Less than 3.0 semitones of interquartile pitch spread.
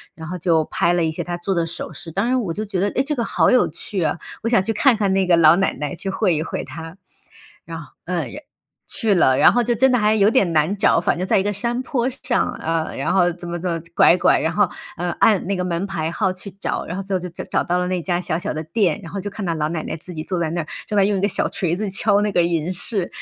No: average, 3.6 semitones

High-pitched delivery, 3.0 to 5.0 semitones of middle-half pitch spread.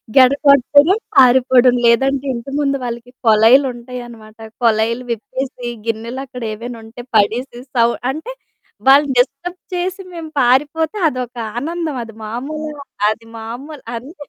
Yes: very high, 255 Hz; average, 3.4 semitones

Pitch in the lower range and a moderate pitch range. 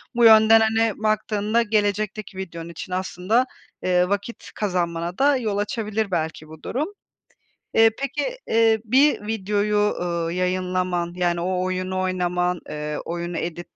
No: high, 190 Hz; average, 3.7 semitones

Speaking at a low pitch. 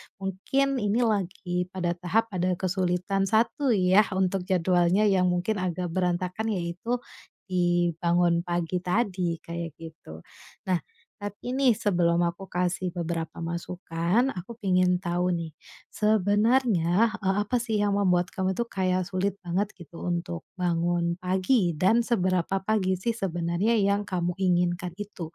No: medium, 185 Hz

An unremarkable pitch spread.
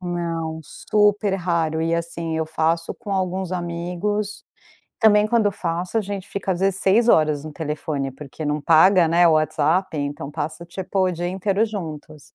Yes: average, 3.4 semitones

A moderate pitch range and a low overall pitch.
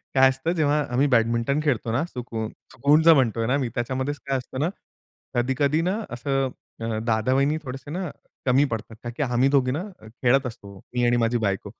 Yes: average, 3.1 semitones; low, 130 Hz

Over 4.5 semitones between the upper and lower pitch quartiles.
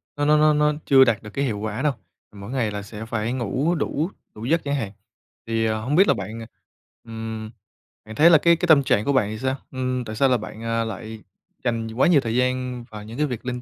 No: average, 4.2 semitones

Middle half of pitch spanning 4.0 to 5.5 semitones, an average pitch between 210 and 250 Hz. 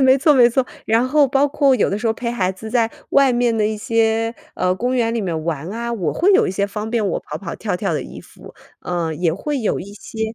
Yes: average, 4.5 semitones; high, 225 Hz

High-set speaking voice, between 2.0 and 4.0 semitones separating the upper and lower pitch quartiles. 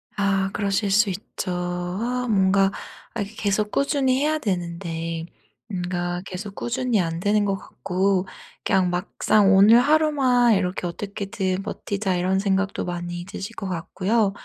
Yes: high, 195 Hz; average, 3.0 semitones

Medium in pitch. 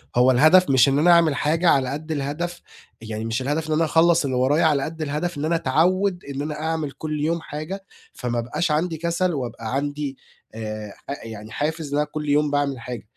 Yes: medium, 150 Hz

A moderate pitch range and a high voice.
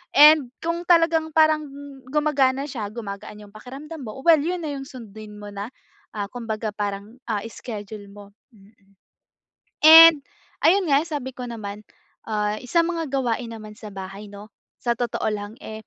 No: wide, 6.4 semitones; high, 235 Hz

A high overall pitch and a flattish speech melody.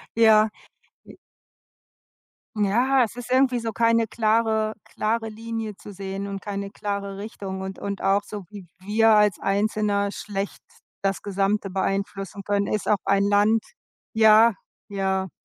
Yes: high, 205 Hz; narrow, 2.0 semitones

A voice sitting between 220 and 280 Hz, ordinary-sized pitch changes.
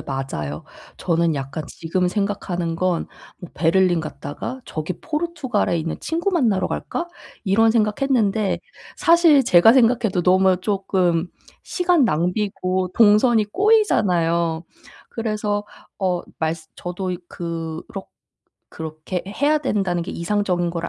No: medium, 185 Hz; average, 4.9 semitones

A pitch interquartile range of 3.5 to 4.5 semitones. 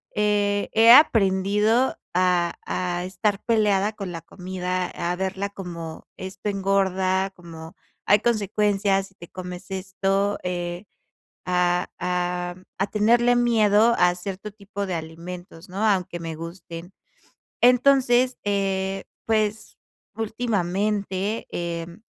No: average, 2.7 semitones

